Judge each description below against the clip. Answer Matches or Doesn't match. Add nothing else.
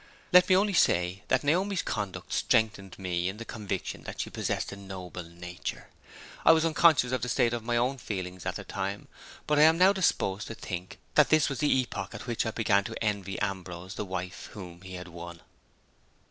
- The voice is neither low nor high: Doesn't match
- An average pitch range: Doesn't match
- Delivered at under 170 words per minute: Doesn't match